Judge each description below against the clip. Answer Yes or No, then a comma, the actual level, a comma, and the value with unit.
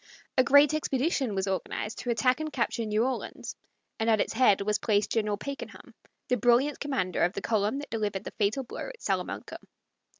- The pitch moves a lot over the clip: No, average, 4.4 semitones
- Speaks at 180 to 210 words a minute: Yes, average, 190 wpm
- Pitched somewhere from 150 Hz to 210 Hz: No, high, 230 Hz